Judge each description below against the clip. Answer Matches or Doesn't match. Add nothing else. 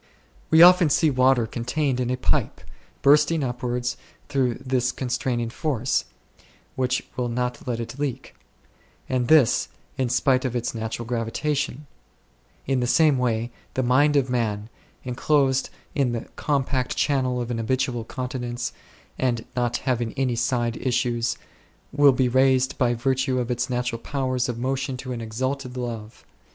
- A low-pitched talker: Matches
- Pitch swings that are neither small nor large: Doesn't match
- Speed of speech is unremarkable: Matches